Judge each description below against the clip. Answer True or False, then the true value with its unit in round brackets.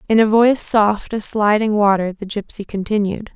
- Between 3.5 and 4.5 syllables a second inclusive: False (5.1 syllables/s)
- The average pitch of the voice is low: False (210 Hz)